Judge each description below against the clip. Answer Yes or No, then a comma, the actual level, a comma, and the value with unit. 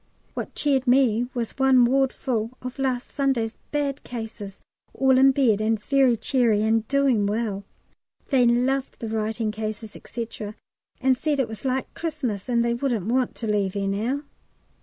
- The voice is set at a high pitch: Yes, high, 240 Hz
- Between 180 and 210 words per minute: No, average, 165 wpm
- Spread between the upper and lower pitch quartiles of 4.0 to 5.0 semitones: No, average, 3.4 semitones